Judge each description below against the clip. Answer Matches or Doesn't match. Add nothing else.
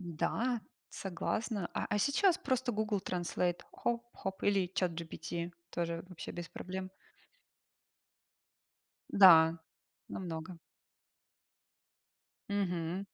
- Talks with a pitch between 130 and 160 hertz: Doesn't match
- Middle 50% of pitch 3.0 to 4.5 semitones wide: Matches